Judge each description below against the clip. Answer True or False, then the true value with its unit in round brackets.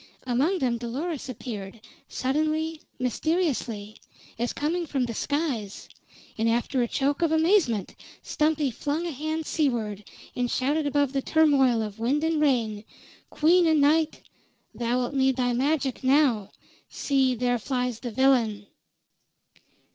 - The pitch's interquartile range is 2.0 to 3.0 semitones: False (4.4 semitones)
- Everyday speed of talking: False (130 wpm)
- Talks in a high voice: True (265 Hz)